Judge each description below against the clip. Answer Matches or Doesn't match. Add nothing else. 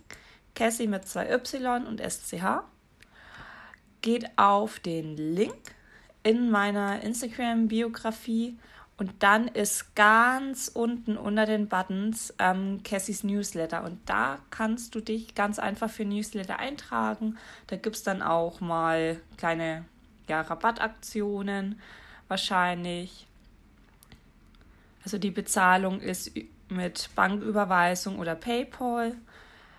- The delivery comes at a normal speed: Doesn't match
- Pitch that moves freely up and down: Doesn't match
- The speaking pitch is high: Matches